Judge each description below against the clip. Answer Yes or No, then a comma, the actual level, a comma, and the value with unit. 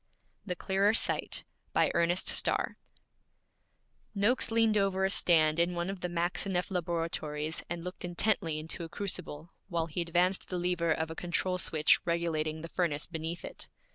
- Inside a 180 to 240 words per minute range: No, average, 160 wpm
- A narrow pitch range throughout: Yes, narrow, 2.1 semitones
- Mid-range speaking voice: Yes, medium, 175 Hz